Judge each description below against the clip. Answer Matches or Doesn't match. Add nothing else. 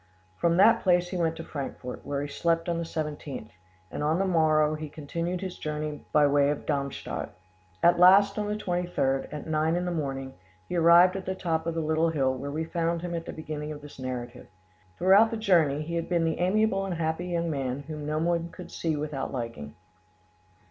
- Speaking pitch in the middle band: Matches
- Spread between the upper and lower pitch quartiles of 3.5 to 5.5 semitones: Doesn't match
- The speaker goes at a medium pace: Doesn't match